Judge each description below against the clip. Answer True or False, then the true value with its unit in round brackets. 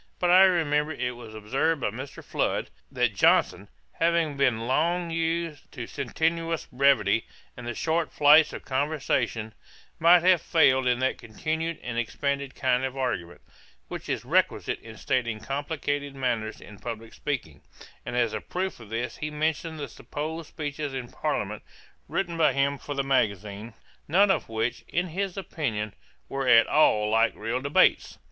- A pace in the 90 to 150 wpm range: False (160 wpm)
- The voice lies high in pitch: False (140 Hz)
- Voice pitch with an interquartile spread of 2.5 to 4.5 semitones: False (5.4 semitones)